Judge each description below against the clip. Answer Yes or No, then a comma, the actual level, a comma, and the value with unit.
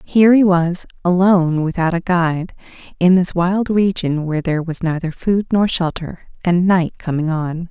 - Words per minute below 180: Yes, average, 170 wpm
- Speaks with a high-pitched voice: No, medium, 175 Hz